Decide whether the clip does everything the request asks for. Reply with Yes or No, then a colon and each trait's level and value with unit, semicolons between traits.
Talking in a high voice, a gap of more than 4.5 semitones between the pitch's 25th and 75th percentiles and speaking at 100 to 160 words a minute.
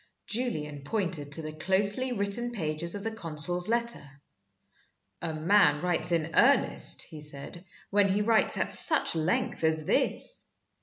No: medium, 175 Hz; average, 5.1 semitones; average, 145 wpm